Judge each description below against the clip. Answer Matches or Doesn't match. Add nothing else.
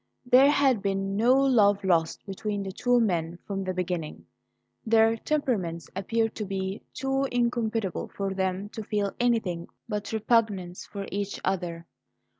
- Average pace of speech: Matches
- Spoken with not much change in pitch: Doesn't match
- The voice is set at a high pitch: Matches